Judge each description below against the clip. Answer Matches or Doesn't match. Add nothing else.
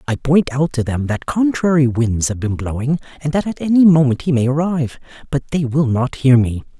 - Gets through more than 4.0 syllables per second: Matches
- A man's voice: Matches